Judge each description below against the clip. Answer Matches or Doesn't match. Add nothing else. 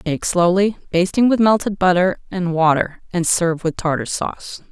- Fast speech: Doesn't match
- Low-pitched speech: Doesn't match